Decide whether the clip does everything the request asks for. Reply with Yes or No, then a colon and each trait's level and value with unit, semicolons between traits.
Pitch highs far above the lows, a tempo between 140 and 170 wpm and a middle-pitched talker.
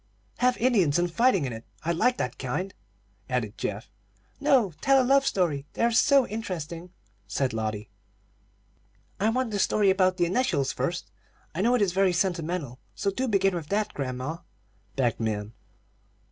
Yes: wide, 8.3 semitones; average, 165 wpm; medium, 180 Hz